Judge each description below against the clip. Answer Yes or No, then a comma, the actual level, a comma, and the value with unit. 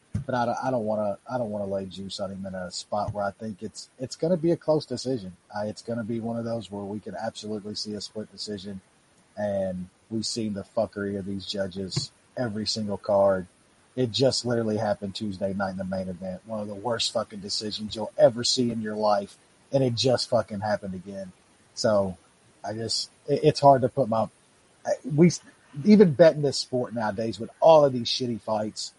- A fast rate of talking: Yes, fast, 215 wpm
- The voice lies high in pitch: No, low, 105 Hz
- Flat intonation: No, average, 3.7 semitones